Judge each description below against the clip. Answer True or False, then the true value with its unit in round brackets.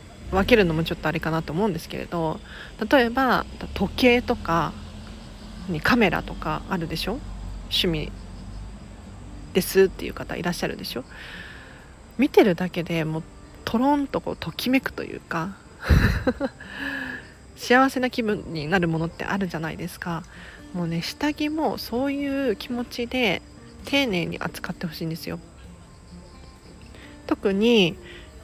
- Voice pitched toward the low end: False (175 Hz)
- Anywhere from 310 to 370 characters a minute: False (275 characters per minute)